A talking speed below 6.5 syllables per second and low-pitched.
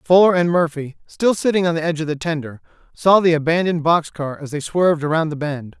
No: 6.1 syllables/s; medium, 160 Hz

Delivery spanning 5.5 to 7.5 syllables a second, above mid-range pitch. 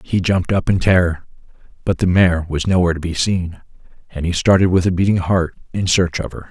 No: 5.8 syllables/s; very low, 90 Hz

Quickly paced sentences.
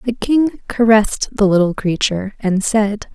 No: average, 155 wpm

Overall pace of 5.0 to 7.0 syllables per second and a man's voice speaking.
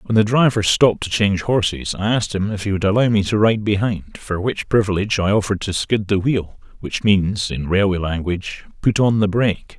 Yes: 5.6 syllables/s; male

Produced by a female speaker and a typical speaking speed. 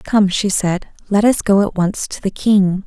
No: female; fast, 230 wpm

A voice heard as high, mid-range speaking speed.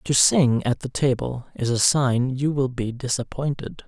No: low, 130 Hz; average, 185 wpm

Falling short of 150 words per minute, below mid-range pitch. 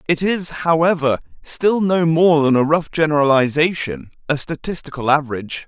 No: slow, 135 wpm; medium, 155 Hz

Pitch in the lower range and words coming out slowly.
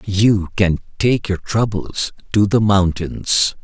Yes: low, 100 Hz; slow, 130 wpm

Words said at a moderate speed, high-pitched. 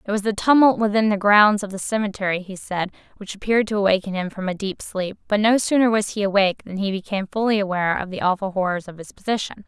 No: fast, 240 wpm; high, 200 Hz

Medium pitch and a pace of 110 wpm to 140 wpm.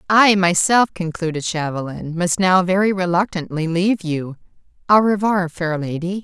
Yes: medium, 180 Hz; slow, 135 wpm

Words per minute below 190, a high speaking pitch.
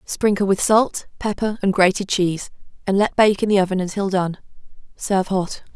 Yes: average, 175 wpm; high, 195 Hz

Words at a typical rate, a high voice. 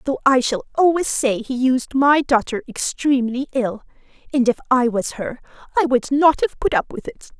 Yes: average, 195 wpm; very high, 260 Hz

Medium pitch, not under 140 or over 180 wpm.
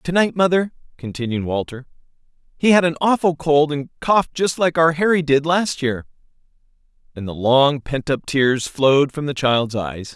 Yes: medium, 145 Hz; average, 170 wpm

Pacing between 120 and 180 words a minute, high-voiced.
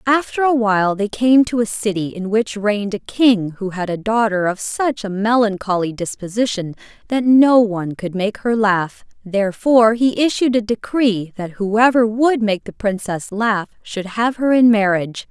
Yes: average, 175 wpm; high, 215 Hz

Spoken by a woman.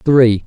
No: male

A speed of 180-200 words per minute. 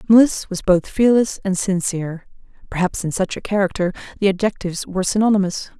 No: average, 155 wpm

